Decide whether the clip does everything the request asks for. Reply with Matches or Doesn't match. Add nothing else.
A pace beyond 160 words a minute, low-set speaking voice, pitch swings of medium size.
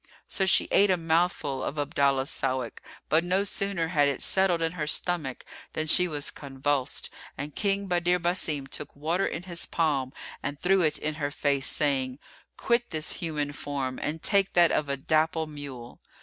Doesn't match